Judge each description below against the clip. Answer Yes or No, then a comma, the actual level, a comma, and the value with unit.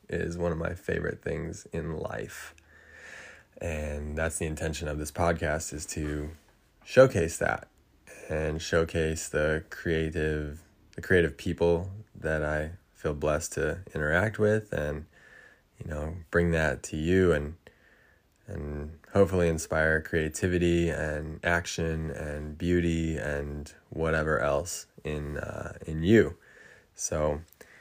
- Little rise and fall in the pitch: Yes, narrow, 2.1 semitones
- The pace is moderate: No, slow, 125 wpm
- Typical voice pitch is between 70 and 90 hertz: Yes, very low, 80 Hz